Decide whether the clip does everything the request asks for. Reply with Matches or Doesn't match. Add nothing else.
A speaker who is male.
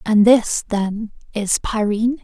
Doesn't match